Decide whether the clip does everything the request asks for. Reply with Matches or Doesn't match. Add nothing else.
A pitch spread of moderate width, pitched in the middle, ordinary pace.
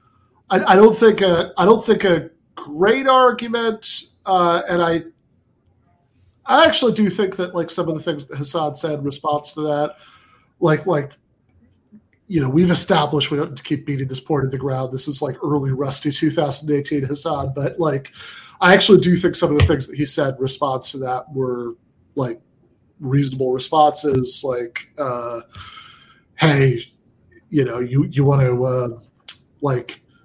Matches